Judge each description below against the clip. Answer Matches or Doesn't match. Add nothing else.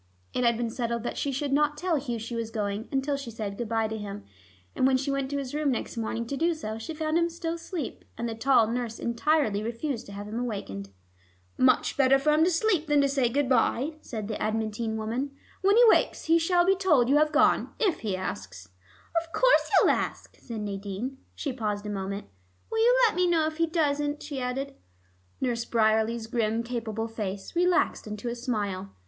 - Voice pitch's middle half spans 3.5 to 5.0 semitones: Doesn't match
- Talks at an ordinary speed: Doesn't match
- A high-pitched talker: Matches